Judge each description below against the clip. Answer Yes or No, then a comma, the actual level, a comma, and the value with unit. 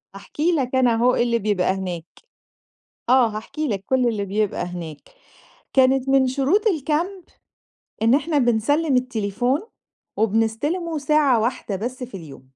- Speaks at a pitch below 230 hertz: No, very high, 250 Hz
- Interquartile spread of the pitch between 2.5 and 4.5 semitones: No, average, 5.0 semitones